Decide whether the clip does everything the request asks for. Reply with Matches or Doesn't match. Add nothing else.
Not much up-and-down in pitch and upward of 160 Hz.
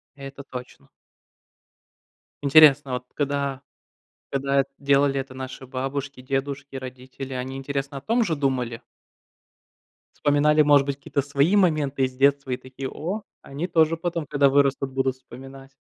Doesn't match